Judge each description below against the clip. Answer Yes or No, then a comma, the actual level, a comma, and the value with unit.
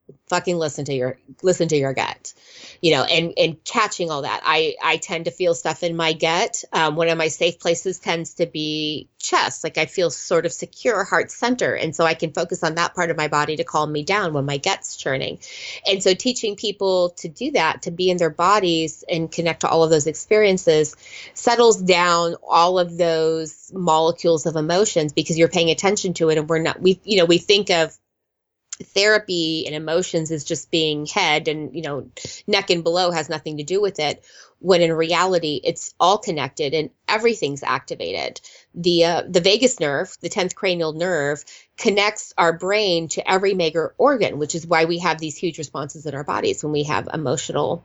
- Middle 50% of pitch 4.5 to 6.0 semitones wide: No, average, 2.7 semitones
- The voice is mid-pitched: Yes, medium, 170 Hz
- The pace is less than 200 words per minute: No, fast, 205 wpm